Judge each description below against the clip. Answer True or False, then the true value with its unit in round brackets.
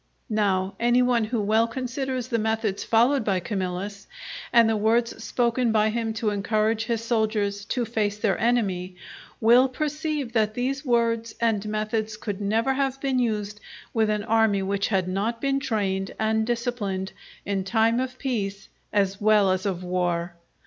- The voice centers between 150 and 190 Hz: False (220 Hz)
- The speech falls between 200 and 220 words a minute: False (165 wpm)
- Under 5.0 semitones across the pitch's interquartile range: True (2.8 semitones)